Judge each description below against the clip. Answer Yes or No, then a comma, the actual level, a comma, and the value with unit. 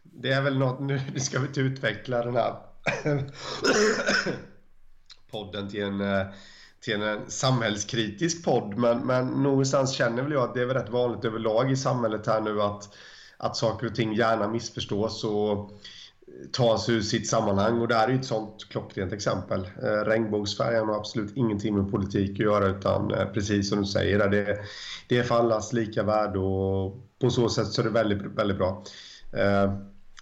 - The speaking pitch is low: Yes, low, 110 Hz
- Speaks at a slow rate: No, average, 175 wpm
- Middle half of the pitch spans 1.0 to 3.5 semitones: Yes, average, 3.1 semitones